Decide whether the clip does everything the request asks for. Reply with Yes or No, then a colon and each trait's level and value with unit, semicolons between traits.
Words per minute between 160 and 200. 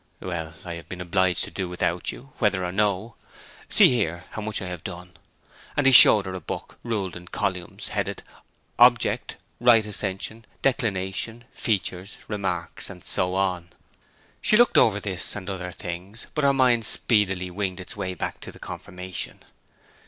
Yes: average, 165 wpm